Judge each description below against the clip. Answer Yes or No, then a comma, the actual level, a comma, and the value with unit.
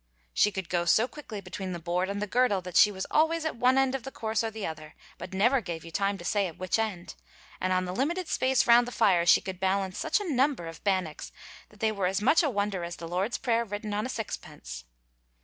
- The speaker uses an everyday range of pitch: Yes, average, 4.8 semitones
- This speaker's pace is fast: Yes, fast, 255 wpm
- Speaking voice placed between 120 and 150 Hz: No, high, 205 Hz